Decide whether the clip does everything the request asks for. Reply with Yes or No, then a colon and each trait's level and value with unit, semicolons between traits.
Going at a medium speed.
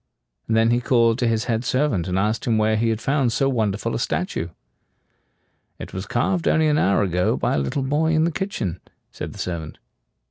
No: fast, 210 wpm